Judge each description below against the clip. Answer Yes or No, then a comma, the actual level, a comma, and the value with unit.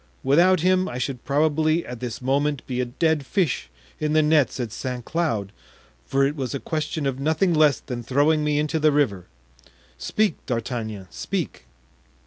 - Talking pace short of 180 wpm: Yes, average, 170 wpm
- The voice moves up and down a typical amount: Yes, average, 3.9 semitones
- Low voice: No, medium, 145 Hz